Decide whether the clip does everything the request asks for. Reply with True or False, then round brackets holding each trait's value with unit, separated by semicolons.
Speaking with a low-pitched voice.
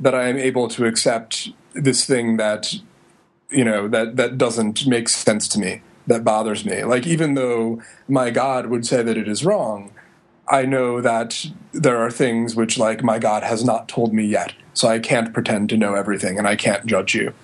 True (115 Hz)